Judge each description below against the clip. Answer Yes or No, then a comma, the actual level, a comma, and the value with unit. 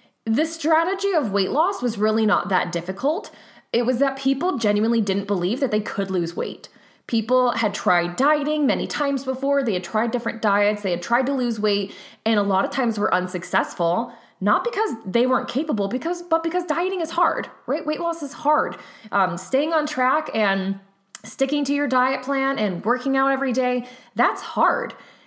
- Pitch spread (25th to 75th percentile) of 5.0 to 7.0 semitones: Yes, wide, 5.5 semitones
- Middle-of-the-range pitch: No, high, 245 Hz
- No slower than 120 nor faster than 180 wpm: No, average, 190 wpm